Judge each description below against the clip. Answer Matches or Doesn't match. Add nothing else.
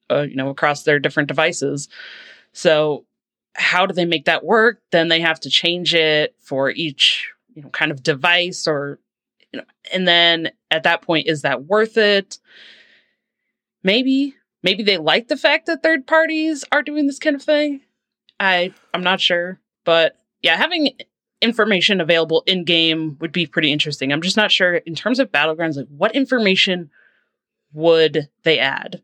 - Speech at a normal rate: Matches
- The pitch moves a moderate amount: Doesn't match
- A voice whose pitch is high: Doesn't match